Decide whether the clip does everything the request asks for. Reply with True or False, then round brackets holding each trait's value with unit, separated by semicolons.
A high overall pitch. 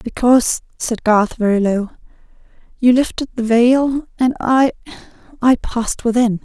True (240 Hz)